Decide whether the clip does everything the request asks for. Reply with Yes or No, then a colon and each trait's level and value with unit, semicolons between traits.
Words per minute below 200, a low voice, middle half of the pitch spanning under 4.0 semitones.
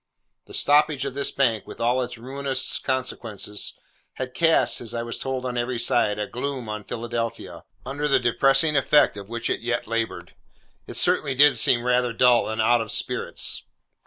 Yes: average, 180 wpm; low, 125 Hz; average, 2.8 semitones